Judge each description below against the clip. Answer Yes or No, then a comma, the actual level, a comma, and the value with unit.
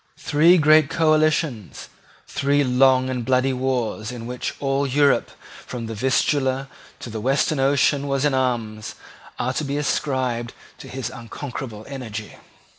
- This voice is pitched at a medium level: No, low, 130 Hz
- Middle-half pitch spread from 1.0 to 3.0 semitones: Yes, average, 2.7 semitones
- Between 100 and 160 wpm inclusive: Yes, average, 140 wpm